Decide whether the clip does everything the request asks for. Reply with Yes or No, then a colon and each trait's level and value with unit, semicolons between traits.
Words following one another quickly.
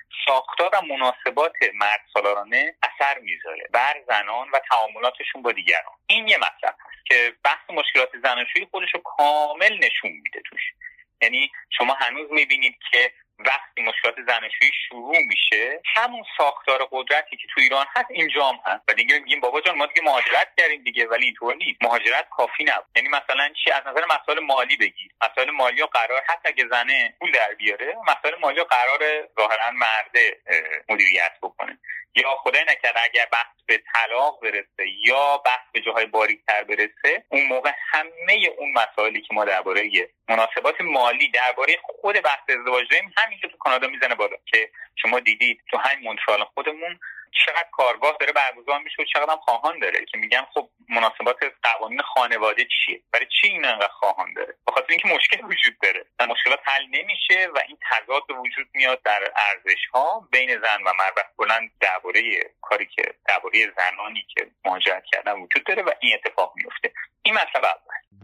Yes: fast, 165 wpm